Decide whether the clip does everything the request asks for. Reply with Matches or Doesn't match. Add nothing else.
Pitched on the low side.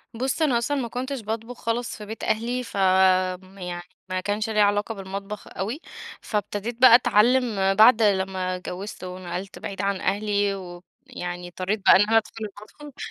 Doesn't match